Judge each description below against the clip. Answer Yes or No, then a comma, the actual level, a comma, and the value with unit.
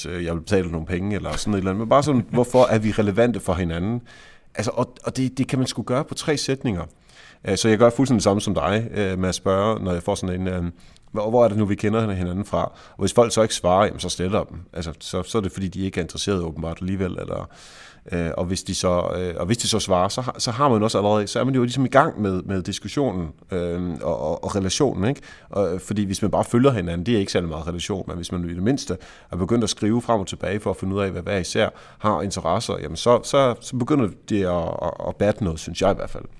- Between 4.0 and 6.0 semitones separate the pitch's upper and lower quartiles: Yes, average, 4.6 semitones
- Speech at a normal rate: No, fast, 270 wpm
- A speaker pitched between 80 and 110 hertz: Yes, low, 100 Hz